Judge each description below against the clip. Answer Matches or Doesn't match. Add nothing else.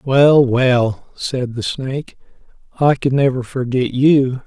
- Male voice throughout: Matches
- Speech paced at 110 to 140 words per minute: Matches